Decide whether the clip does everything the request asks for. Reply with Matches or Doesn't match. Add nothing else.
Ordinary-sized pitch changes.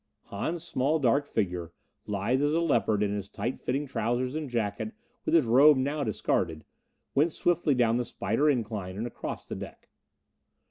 Doesn't match